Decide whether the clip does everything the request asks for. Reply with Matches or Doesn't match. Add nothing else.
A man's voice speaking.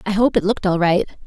Doesn't match